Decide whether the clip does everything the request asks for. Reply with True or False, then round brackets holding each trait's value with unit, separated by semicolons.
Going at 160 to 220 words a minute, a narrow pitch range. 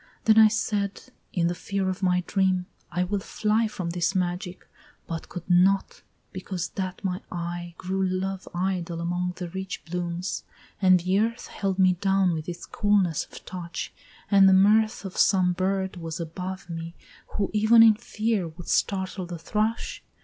True (170 wpm; 2.0 semitones)